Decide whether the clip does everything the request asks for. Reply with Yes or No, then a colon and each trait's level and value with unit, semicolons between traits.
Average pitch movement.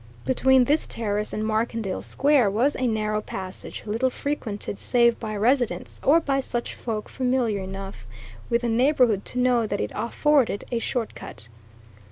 Yes: average, 3.4 semitones